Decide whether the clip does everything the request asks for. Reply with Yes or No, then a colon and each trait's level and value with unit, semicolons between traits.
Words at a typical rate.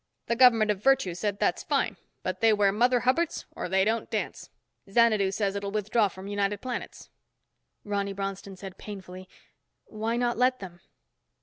Yes: average, 165 wpm